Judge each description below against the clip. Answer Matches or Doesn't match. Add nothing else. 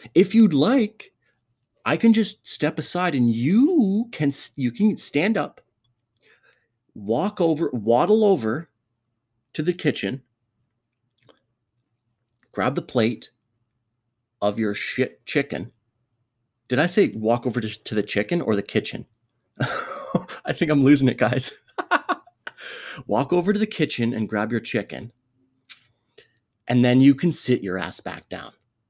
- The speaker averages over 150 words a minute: Doesn't match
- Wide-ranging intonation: Matches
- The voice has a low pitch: Matches